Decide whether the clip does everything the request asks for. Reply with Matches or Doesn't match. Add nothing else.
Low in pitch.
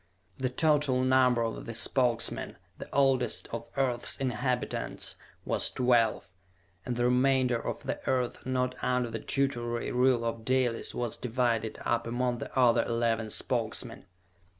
Matches